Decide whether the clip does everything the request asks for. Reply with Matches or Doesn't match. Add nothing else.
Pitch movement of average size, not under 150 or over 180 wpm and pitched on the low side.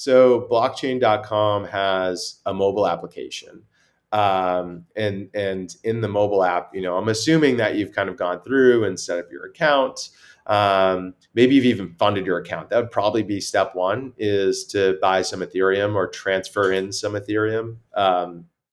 Matches